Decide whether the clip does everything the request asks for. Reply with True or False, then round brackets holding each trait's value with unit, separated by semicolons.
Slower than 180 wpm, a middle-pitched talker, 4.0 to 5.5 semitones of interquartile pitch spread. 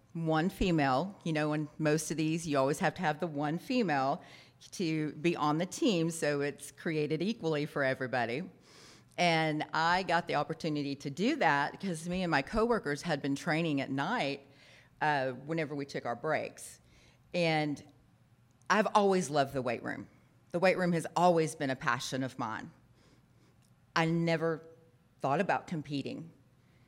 False (165 wpm; 155 Hz; 3.3 semitones)